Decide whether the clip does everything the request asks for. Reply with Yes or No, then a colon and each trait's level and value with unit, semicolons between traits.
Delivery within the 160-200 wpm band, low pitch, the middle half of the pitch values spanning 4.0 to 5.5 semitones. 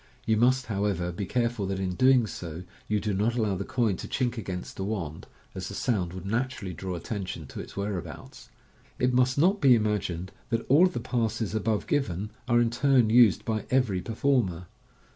Yes: average, 195 wpm; low, 110 Hz; average, 4.5 semitones